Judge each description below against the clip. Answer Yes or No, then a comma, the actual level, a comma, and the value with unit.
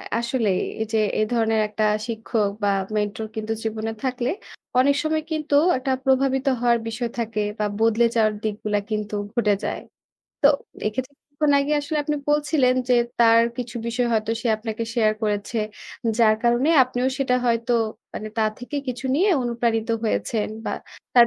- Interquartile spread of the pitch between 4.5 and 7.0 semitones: No, average, 2.9 semitones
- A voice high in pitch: Yes, high, 235 Hz